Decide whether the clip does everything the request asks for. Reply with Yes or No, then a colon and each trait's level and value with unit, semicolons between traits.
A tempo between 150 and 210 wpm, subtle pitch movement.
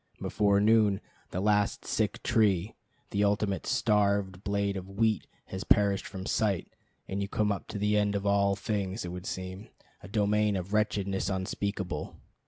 Yes: average, 160 wpm; narrow, 1.4 semitones